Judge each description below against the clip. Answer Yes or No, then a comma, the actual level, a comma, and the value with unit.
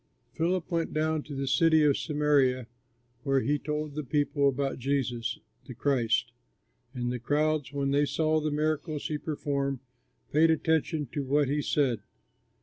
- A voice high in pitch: No, medium, 145 Hz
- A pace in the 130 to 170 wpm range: Yes, average, 155 wpm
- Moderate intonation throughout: No, narrow, 2.1 semitones